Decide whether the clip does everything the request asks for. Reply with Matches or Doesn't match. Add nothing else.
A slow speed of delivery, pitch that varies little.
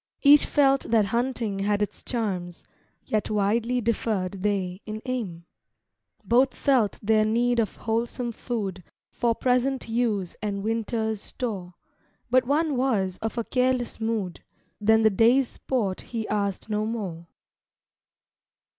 Doesn't match